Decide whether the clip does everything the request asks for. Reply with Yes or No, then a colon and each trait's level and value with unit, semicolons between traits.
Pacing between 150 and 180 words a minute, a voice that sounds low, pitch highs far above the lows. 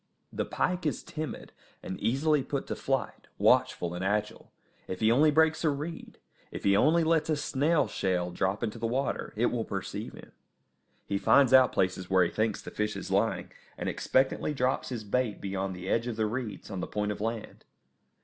No: average, 195 wpm; low, 115 Hz; wide, 6.5 semitones